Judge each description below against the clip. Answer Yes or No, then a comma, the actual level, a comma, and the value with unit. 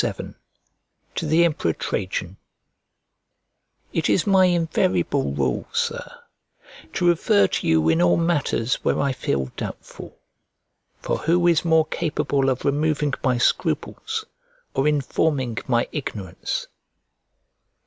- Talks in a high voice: No, medium, 140 Hz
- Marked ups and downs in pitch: Yes, wide, 8.9 semitones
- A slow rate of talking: Yes, slow, 120 wpm